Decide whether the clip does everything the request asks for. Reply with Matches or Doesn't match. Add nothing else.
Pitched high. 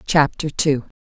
Doesn't match